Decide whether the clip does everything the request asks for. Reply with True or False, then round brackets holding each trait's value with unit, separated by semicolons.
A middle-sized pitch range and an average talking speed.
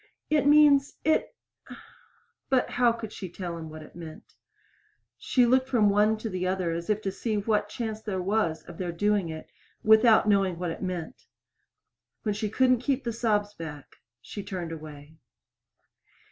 True (4.7 semitones; 170 wpm)